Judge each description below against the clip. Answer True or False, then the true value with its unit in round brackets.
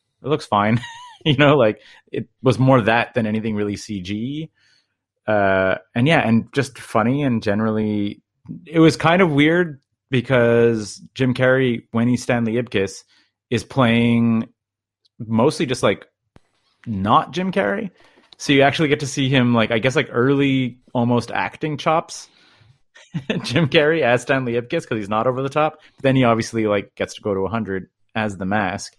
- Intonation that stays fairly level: False (4.0 semitones)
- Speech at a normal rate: True (170 wpm)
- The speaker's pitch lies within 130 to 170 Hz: False (120 Hz)